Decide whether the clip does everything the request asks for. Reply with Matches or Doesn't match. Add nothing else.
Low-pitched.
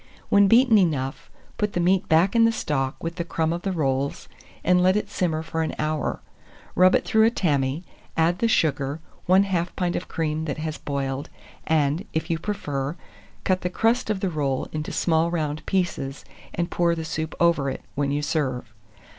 Doesn't match